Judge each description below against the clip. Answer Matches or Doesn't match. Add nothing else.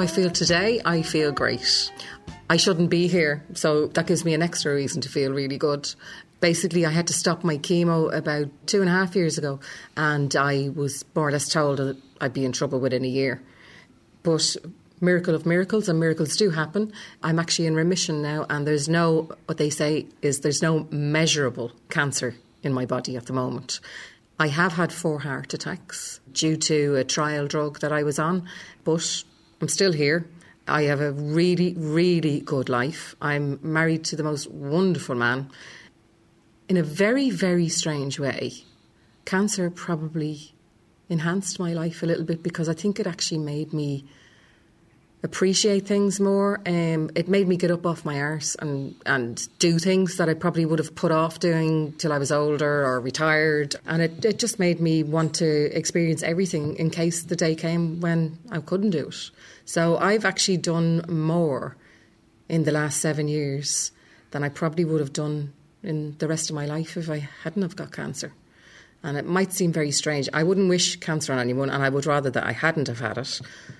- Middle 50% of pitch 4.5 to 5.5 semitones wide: Doesn't match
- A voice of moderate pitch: Matches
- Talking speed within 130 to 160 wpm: Doesn't match